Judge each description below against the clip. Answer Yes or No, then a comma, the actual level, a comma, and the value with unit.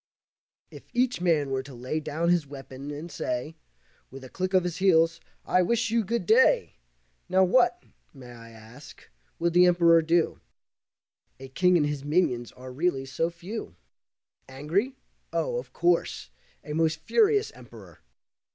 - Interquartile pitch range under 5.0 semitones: No, average, 5.3 semitones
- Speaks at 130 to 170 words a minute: Yes, average, 155 wpm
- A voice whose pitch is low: No, medium, 165 Hz